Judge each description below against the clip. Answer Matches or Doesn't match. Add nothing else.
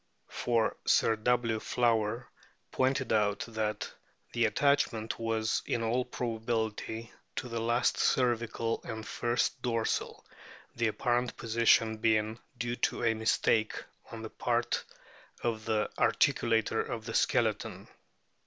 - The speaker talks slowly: Matches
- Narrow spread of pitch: Matches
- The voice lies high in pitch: Doesn't match